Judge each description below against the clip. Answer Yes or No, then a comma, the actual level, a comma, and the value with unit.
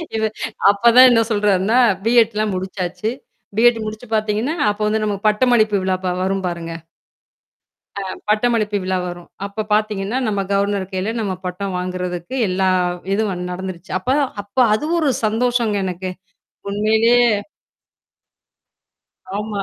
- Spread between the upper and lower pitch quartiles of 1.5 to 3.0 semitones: Yes, average, 2.7 semitones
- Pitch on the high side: Yes, high, 210 Hz